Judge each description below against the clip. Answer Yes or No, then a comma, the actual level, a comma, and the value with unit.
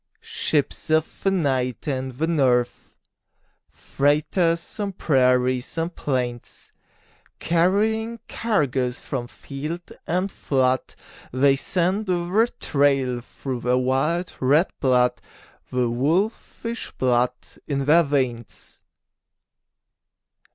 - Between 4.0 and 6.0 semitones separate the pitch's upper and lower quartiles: Yes, average, 5.2 semitones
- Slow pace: Yes, slow, 95 wpm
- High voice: No, medium, 140 Hz